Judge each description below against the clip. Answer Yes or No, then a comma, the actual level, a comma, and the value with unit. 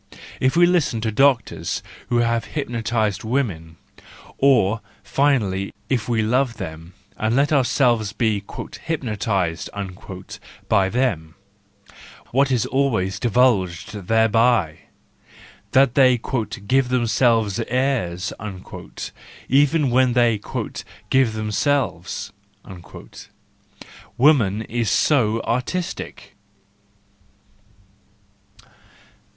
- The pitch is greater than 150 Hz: No, low, 115 Hz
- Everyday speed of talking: No, slow, 85 wpm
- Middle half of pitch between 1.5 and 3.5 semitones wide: No, average, 4.4 semitones